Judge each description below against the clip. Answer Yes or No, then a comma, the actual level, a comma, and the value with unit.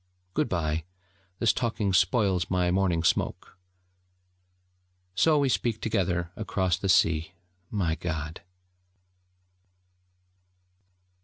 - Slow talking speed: Yes, slow, 90 wpm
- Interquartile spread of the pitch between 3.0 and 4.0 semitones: Yes, average, 3.6 semitones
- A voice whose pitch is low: Yes, very low, 90 Hz